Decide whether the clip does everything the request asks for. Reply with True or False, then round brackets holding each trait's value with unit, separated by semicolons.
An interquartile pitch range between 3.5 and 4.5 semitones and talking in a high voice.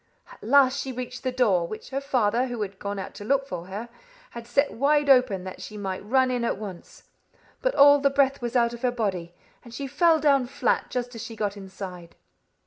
False (4.9 semitones; 240 Hz)